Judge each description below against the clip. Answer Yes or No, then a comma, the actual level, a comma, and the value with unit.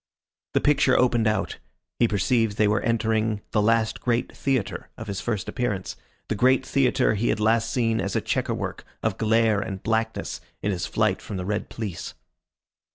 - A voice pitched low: Yes, low, 110 Hz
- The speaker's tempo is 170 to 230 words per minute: Yes, average, 175 wpm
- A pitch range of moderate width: No, narrow, 2.1 semitones